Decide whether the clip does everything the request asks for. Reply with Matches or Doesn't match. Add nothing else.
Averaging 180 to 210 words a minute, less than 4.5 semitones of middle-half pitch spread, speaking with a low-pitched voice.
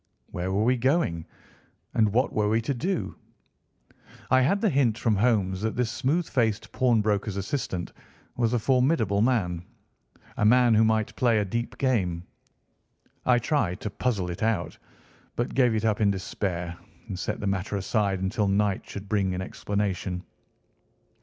Doesn't match